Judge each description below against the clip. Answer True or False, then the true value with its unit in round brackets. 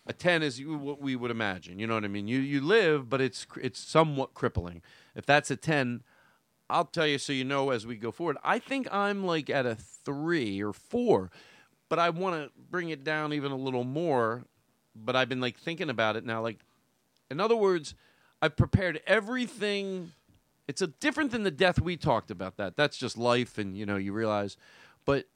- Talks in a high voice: False (135 Hz)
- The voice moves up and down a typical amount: False (6.7 semitones)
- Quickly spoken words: True (210 wpm)